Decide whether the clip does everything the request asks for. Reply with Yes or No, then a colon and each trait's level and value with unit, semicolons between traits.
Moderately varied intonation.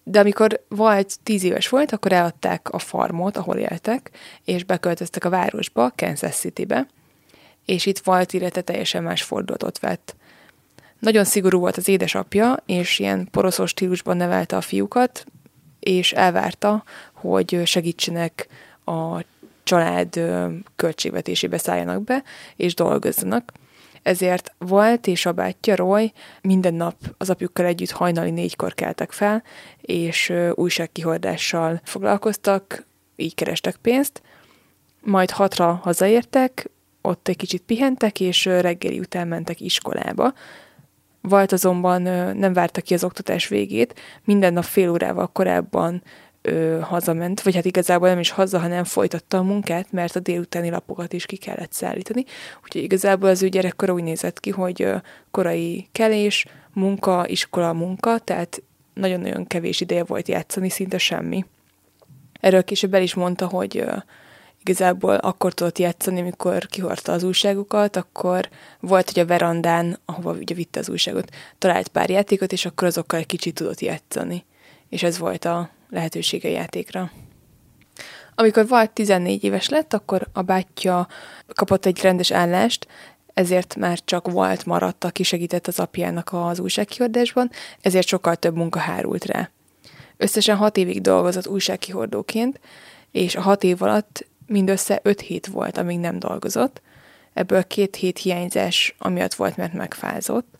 No: narrow, 2.3 semitones